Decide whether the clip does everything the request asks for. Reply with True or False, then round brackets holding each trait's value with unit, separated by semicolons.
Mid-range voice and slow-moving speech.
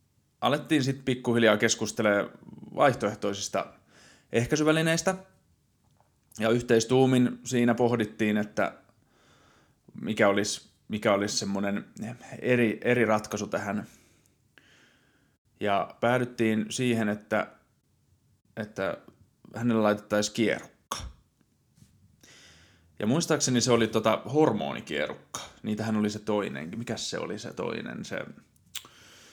False (115 Hz; 90 wpm)